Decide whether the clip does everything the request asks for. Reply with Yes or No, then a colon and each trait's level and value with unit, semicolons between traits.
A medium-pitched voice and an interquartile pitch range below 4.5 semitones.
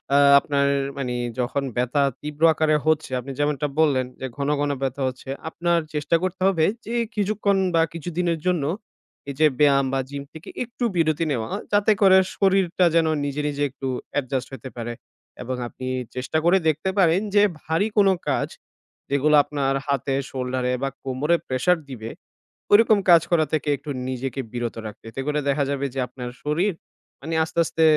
Yes: medium, 150 Hz; average, 4.0 semitones